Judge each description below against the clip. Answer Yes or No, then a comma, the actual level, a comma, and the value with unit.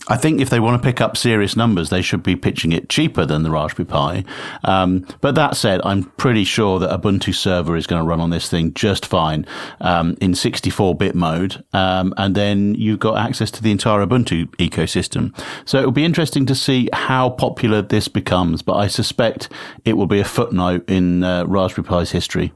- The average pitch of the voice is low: Yes, low, 100 Hz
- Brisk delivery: Yes, fast, 210 wpm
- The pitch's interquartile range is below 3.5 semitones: No, average, 4.1 semitones